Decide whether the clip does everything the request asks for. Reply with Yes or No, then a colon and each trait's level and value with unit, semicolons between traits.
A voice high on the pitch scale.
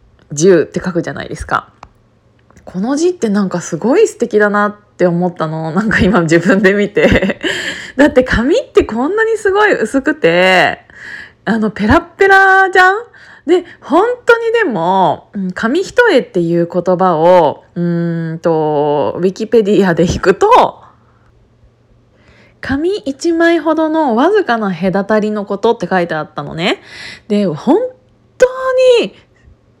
Yes: high, 225 Hz